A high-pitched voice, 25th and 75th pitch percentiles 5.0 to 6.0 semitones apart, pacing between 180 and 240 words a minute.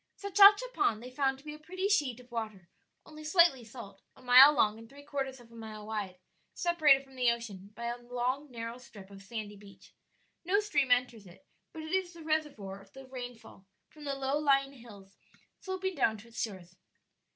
Yes: very high, 250 Hz; wide, 5.4 semitones; average, 200 wpm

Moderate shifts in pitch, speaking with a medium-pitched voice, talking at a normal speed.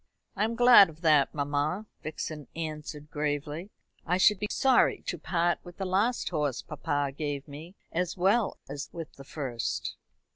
Yes: average, 4.2 semitones; medium, 160 Hz; average, 160 wpm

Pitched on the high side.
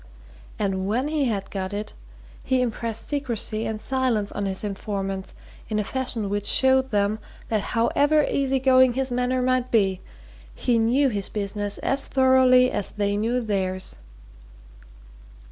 Yes: high, 230 Hz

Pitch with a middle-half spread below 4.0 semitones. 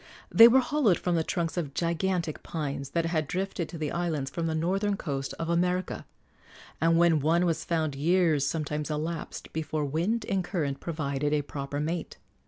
Yes: average, 2.9 semitones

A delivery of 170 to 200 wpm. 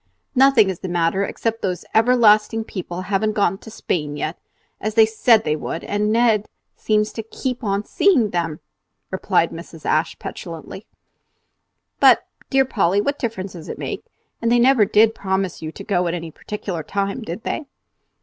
Yes: average, 175 wpm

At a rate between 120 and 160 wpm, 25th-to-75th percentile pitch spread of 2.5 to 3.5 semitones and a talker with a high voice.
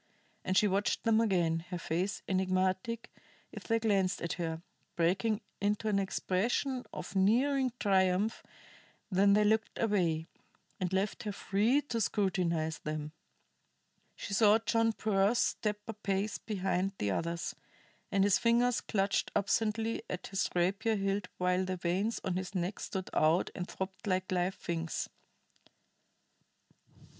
Yes: average, 140 wpm; average, 2.9 semitones; high, 195 Hz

